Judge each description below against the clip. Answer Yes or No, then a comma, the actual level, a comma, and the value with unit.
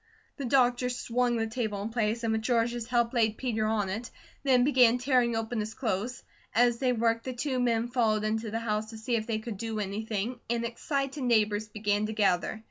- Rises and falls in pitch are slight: Yes, narrow, 2.2 semitones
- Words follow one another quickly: Yes, fast, 210 wpm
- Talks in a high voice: Yes, high, 230 Hz